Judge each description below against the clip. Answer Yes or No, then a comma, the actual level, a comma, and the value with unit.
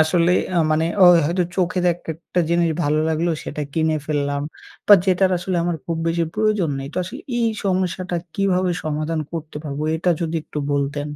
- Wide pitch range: No, average, 2.9 semitones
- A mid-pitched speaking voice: Yes, medium, 170 Hz